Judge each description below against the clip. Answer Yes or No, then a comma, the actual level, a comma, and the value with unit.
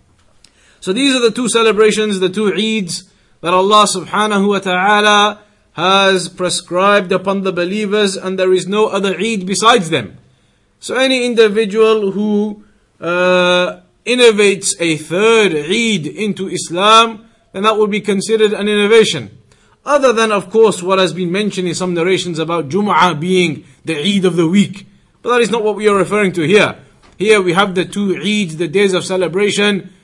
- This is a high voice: Yes, high, 195 Hz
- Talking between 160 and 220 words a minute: Yes, average, 170 wpm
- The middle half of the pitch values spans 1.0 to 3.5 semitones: Yes, average, 2.9 semitones